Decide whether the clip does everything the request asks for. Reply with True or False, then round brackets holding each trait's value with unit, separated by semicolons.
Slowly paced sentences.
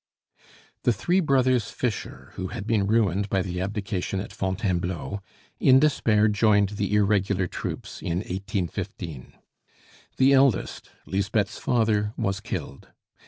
True (120 wpm)